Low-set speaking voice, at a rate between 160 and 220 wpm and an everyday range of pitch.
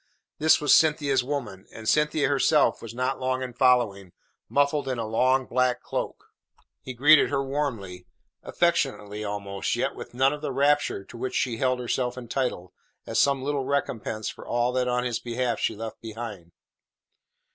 Yes: low, 125 Hz; average, 170 wpm; average, 3.5 semitones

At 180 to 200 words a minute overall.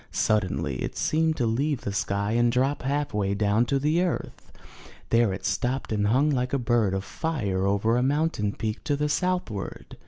Yes: average, 190 wpm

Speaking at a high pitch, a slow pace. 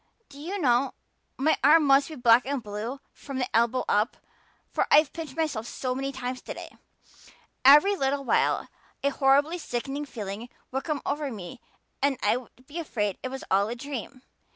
No: very high, 270 Hz; average, 175 wpm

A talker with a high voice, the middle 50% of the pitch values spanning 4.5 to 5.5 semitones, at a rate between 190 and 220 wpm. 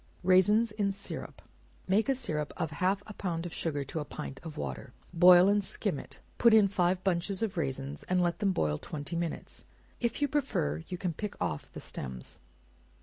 No: medium, 180 Hz; average, 5.0 semitones; average, 195 wpm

